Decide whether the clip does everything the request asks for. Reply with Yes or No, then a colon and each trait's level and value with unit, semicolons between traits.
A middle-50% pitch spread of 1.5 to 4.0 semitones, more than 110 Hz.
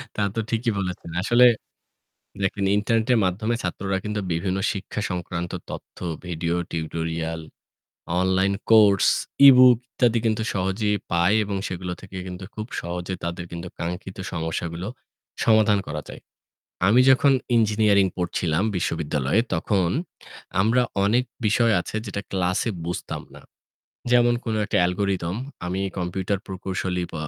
No: average, 3.5 semitones; very low, 95 Hz